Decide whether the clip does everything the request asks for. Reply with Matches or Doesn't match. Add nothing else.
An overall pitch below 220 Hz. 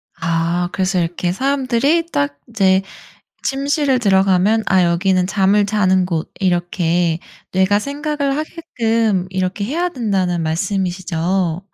Matches